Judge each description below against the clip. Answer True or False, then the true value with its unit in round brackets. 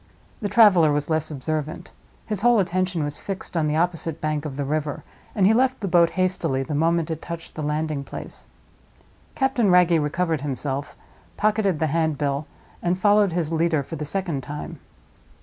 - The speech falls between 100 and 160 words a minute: False (175 wpm)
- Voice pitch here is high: False (165 Hz)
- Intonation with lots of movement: False (3.8 semitones)